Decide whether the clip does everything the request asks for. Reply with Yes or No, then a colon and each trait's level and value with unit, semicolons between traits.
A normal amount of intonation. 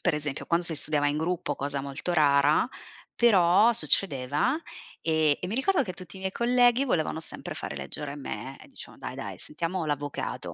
Yes: average, 4.9 semitones